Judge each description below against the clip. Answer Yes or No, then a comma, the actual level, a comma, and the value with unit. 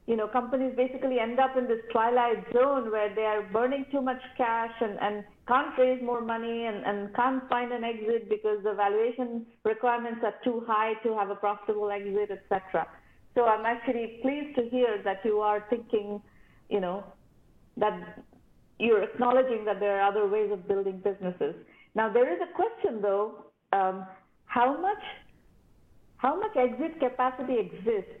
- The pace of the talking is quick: No, average, 170 wpm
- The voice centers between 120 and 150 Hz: No, high, 230 Hz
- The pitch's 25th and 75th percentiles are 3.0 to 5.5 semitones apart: Yes, average, 3.3 semitones